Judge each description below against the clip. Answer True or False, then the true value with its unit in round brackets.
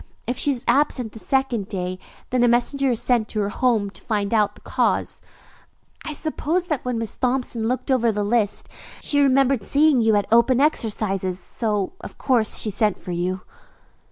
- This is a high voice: True (235 Hz)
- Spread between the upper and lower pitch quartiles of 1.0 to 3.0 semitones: False (4.3 semitones)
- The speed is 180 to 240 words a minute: True (185 wpm)